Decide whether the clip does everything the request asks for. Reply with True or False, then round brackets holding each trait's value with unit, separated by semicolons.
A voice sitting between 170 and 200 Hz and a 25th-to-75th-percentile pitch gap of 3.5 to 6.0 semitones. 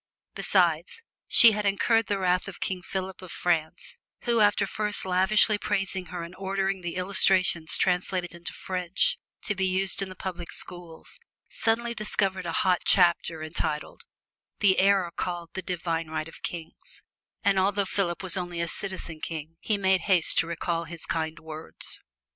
False (185 Hz; 2.5 semitones)